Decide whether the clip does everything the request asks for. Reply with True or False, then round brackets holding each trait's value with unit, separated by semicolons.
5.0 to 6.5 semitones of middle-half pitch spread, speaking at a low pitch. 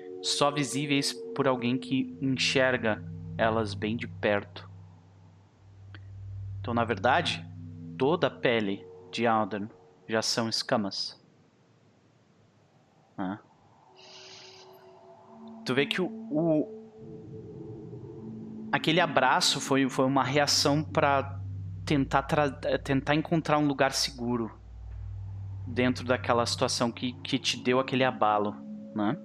True (5.6 semitones; 115 Hz)